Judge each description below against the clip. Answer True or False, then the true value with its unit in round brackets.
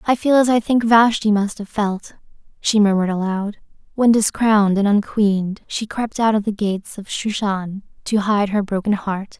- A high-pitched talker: True (210 Hz)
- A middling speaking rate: True (185 wpm)